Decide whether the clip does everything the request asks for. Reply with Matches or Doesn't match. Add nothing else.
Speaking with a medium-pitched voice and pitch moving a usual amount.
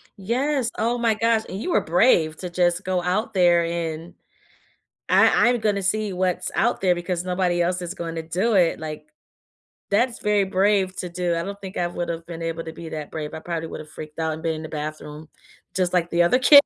Matches